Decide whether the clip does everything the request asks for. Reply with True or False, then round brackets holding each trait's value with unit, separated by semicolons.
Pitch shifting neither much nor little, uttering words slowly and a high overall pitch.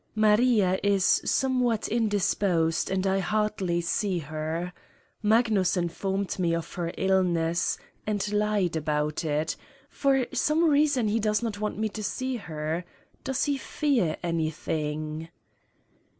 True (4.6 semitones; 125 wpm; 195 Hz)